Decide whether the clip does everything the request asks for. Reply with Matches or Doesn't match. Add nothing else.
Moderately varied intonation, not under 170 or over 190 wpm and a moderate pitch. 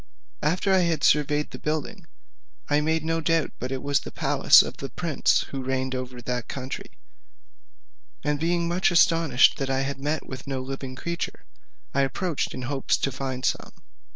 Matches